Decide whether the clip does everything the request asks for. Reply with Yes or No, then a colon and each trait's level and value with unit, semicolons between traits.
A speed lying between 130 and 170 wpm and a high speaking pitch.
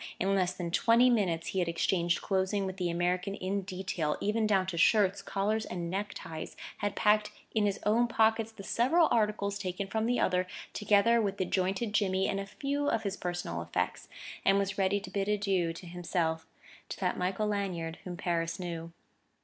No: average, 190 wpm; high, 195 Hz